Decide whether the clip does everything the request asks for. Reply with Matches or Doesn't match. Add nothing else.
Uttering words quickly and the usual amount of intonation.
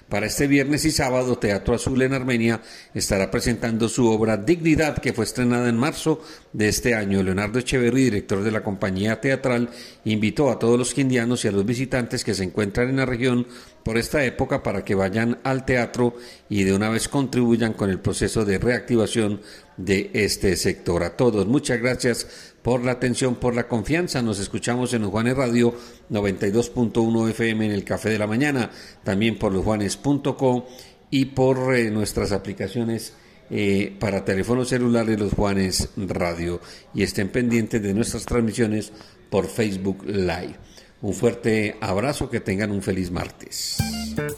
Doesn't match